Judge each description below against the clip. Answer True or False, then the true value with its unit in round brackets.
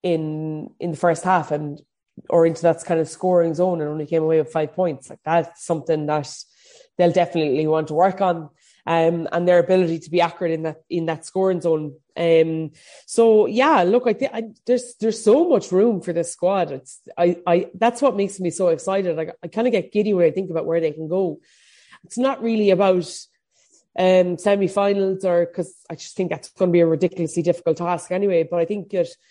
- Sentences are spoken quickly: True (215 wpm)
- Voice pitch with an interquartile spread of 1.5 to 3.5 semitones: True (2.8 semitones)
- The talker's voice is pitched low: False (175 Hz)